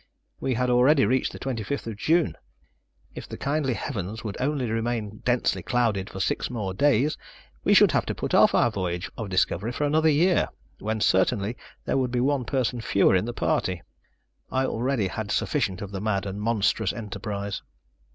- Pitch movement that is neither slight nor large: Yes, average, 4.6 semitones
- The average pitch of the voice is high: No, low, 115 Hz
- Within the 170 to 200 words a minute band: Yes, average, 180 wpm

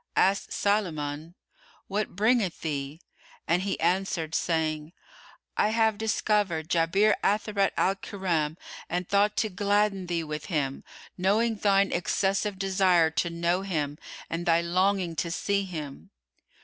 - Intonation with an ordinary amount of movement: Yes, average, 3.6 semitones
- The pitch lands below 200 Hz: Yes, medium, 185 Hz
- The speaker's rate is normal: No, slow, 130 wpm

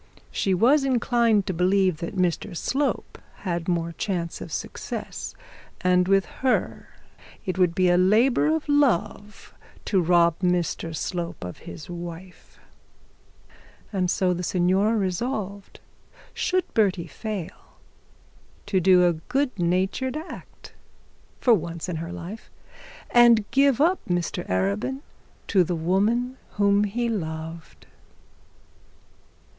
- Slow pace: Yes, slow, 120 wpm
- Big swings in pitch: No, average, 4.7 semitones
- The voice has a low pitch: No, medium, 185 Hz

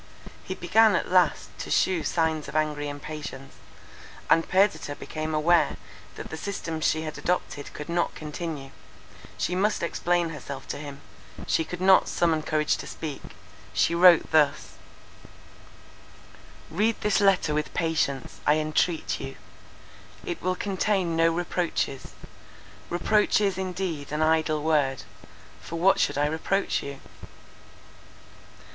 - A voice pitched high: No, medium, 160 Hz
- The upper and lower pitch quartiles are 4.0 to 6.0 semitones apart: No, average, 3.1 semitones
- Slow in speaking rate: Yes, slow, 130 wpm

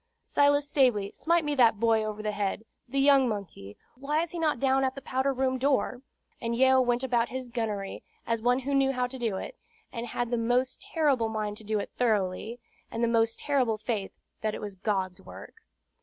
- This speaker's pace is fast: Yes, fast, 210 wpm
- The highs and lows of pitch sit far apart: No, average, 3.7 semitones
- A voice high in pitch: Yes, high, 245 Hz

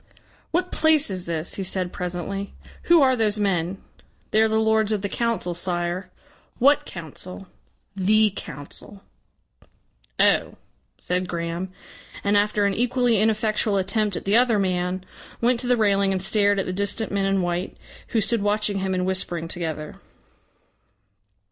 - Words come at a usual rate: Yes, average, 155 wpm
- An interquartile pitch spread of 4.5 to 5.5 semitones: No, average, 3.2 semitones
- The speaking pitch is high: Yes, high, 200 Hz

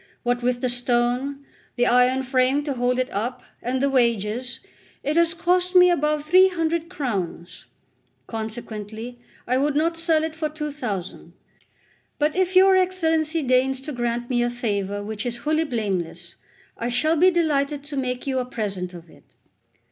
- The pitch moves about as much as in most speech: Yes, average, 4.6 semitones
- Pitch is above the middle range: Yes, very high, 255 Hz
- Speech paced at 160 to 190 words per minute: Yes, average, 170 wpm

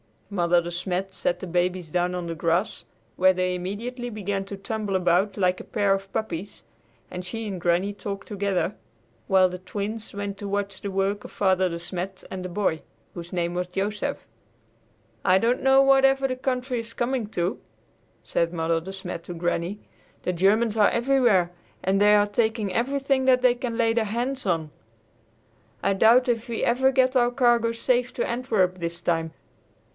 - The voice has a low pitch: No, high, 200 Hz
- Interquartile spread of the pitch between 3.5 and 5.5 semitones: Yes, average, 4.4 semitones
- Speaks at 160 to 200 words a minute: Yes, average, 180 wpm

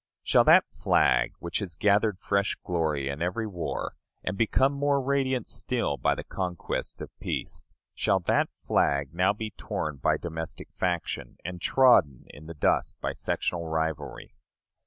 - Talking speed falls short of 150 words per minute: No, average, 155 wpm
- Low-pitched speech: Yes, very low, 90 Hz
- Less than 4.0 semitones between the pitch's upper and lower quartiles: No, average, 4.8 semitones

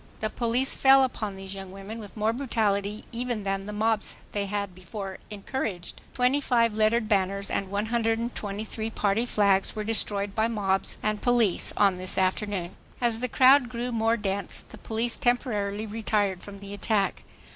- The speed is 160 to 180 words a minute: Yes, average, 165 wpm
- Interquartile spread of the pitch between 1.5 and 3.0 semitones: Yes, average, 2.7 semitones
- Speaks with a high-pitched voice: Yes, high, 215 Hz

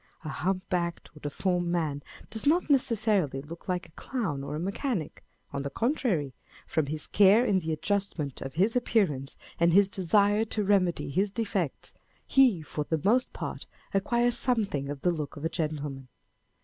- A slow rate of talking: No, average, 175 wpm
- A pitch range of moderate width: No, wide, 5.8 semitones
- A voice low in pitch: No, medium, 180 Hz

